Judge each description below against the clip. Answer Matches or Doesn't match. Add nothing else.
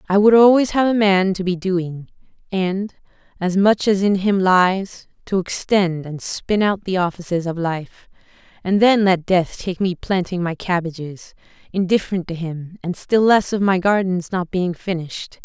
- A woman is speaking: Matches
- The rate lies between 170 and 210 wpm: Matches